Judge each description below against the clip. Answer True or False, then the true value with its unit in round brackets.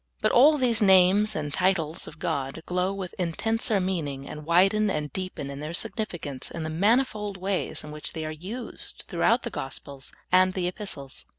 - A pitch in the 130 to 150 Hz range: False (180 Hz)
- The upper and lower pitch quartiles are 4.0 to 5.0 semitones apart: True (4.7 semitones)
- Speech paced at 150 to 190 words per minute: True (180 wpm)